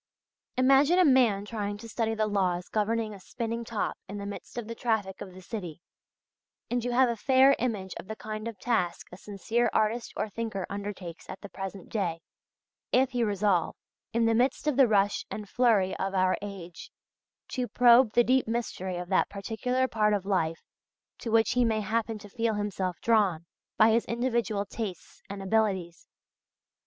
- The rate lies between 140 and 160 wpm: No, average, 185 wpm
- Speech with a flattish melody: No, average, 3.1 semitones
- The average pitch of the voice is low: No, high, 215 Hz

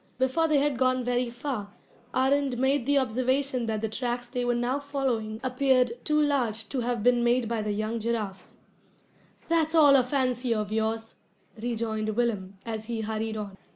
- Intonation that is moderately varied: Yes, average, 3.0 semitones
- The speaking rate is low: No, average, 175 wpm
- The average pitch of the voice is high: Yes, high, 245 Hz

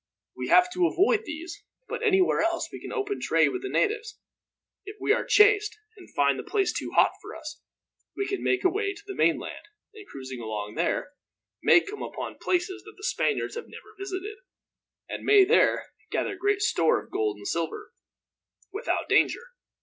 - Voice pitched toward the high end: Yes, very high, 390 Hz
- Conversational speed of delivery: Yes, average, 180 wpm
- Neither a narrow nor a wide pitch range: Yes, average, 4.0 semitones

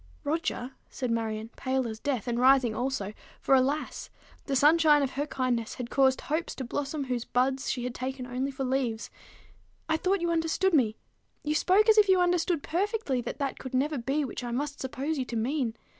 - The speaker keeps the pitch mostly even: No, average, 3.7 semitones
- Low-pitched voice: No, very high, 270 Hz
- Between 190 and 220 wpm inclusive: Yes, average, 200 wpm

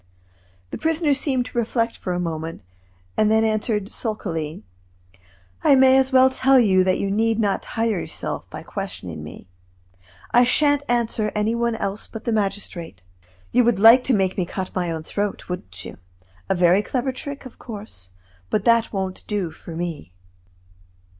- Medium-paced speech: Yes, average, 175 wpm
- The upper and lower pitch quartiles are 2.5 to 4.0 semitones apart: No, average, 4.6 semitones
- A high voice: Yes, high, 215 Hz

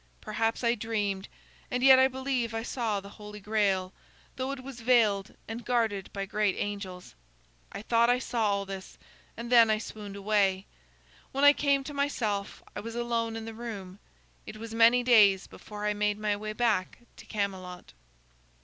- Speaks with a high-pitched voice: Yes, high, 220 Hz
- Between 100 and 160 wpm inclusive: No, average, 175 wpm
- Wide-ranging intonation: No, average, 2.9 semitones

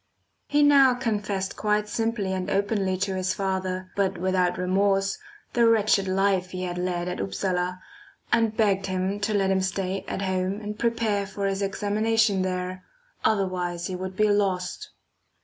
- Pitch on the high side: Yes, high, 195 Hz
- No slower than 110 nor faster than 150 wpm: No, average, 160 wpm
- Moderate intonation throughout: No, narrow, 2.1 semitones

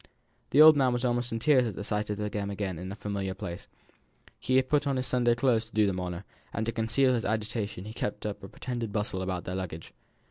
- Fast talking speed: Yes, fast, 245 wpm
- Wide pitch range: No, average, 3.7 semitones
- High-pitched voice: No, low, 110 Hz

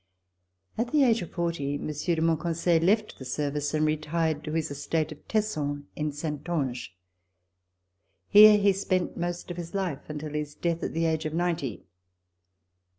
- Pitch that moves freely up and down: No, average, 2.9 semitones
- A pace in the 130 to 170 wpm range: Yes, average, 160 wpm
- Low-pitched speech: No, medium, 160 Hz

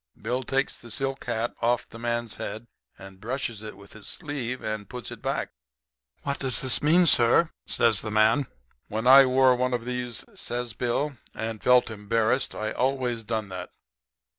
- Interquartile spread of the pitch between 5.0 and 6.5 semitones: No, average, 2.9 semitones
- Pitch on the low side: Yes, low, 120 Hz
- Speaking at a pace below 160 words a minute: No, average, 175 wpm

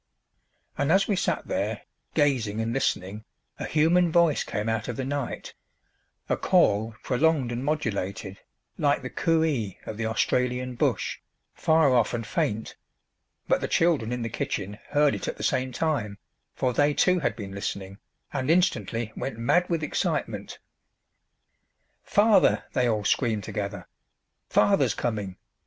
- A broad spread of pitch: Yes, wide, 5.7 semitones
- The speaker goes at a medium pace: Yes, average, 150 wpm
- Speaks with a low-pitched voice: Yes, low, 125 Hz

